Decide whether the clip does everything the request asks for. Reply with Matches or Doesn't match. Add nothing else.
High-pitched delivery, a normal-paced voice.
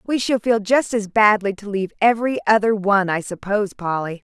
Matches